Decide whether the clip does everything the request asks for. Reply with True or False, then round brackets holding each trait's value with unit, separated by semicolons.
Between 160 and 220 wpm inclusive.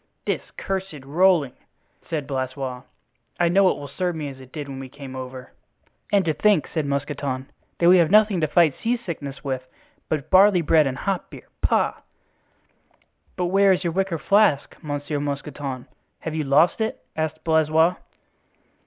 True (165 wpm)